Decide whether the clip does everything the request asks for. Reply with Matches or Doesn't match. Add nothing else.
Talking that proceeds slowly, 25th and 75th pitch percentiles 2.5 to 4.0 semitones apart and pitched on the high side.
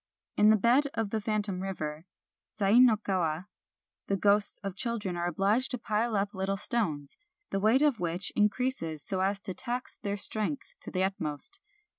Doesn't match